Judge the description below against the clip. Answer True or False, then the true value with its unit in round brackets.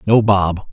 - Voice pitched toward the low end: True (100 Hz)